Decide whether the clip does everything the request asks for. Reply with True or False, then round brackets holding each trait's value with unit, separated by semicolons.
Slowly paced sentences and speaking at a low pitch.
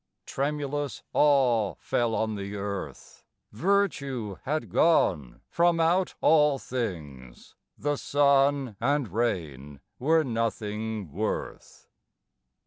True (95 wpm; 125 Hz)